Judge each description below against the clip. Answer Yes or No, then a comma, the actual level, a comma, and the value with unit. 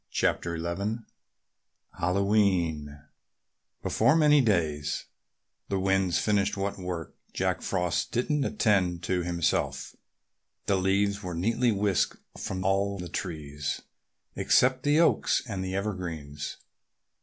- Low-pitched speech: Yes, very low, 95 Hz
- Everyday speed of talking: No, slow, 110 wpm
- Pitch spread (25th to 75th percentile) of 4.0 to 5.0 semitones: No, average, 3.4 semitones